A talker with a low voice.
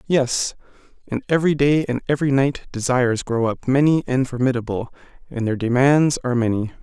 Yes: low, 130 Hz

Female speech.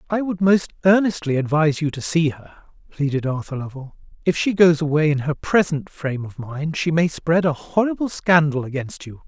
No: male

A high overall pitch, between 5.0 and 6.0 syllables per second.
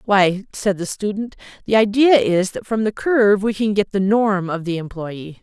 No: high, 200 Hz; 4.7 syllables/s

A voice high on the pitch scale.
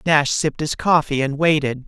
No: medium, 150 Hz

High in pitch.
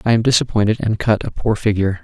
No: low, 110 Hz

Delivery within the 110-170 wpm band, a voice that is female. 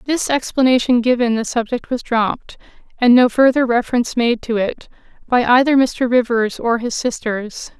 Yes: average, 160 wpm; female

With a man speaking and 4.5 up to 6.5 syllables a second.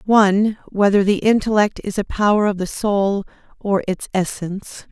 No: female; 5.1 syllables/s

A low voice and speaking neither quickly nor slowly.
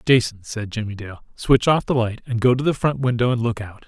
No: low, 115 Hz; fast, 265 wpm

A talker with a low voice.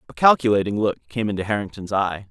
Yes: low, 105 Hz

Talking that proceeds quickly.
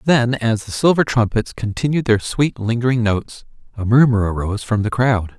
No: average, 180 wpm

